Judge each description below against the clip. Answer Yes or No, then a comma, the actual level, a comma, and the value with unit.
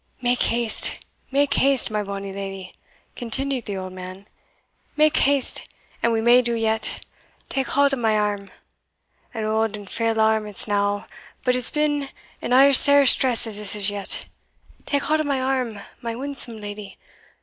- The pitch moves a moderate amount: Yes, average, 4.6 semitones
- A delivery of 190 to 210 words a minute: No, average, 170 wpm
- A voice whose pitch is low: No, high, 230 Hz